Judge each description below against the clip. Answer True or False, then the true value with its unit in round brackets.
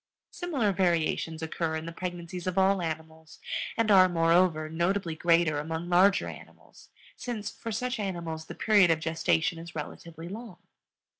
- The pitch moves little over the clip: False (3.1 semitones)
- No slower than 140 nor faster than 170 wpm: True (150 wpm)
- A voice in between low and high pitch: True (170 Hz)